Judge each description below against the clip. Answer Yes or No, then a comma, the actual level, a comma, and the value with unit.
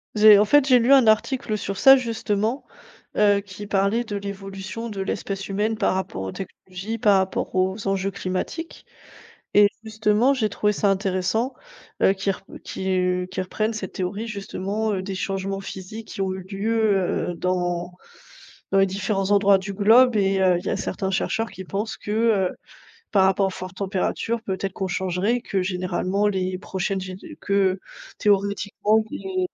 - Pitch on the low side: No, high, 200 Hz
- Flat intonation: Yes, narrow, 2.2 semitones